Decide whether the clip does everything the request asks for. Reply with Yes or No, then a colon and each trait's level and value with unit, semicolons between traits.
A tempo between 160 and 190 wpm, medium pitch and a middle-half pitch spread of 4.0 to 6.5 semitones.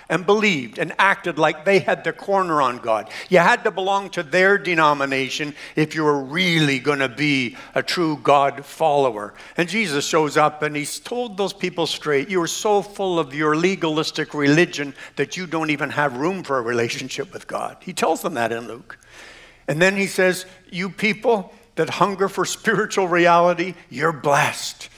Yes: average, 180 wpm; medium, 165 Hz; average, 4.5 semitones